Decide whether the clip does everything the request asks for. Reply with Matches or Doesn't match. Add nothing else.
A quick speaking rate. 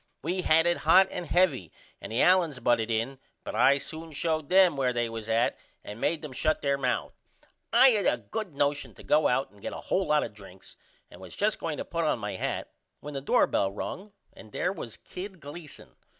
Matches